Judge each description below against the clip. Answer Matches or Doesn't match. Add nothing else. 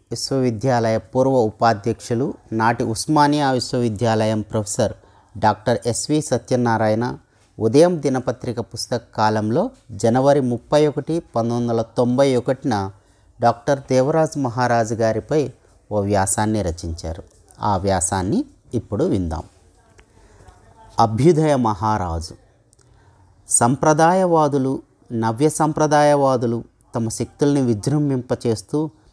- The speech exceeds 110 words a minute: Doesn't match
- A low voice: Matches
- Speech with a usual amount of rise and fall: Matches